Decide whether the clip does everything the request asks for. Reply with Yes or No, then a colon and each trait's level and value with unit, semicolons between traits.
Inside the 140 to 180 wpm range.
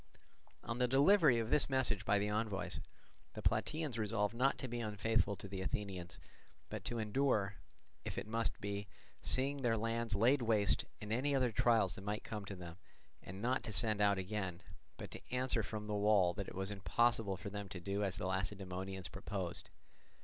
No: average, 190 wpm